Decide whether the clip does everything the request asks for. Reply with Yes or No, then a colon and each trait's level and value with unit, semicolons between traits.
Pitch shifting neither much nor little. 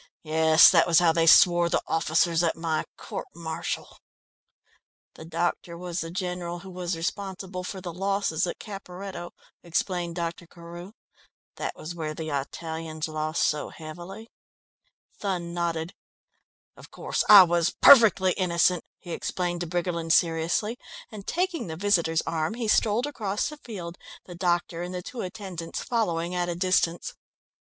No: narrow, 2.3 semitones